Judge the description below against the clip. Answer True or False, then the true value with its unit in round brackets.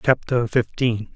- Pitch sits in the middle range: False (115 Hz)